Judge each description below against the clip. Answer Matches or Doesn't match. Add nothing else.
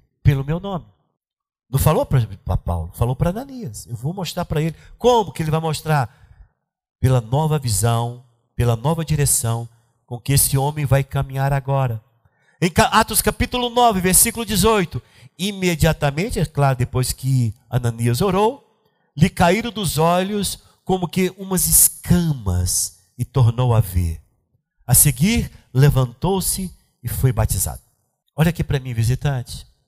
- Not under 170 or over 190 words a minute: Doesn't match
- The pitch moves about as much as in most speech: Doesn't match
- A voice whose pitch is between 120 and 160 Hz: Matches